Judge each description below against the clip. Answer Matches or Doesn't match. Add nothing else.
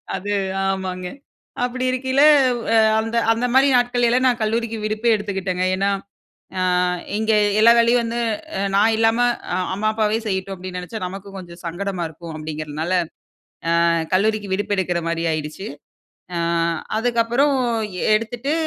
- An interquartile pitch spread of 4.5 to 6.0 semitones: Doesn't match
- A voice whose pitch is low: Doesn't match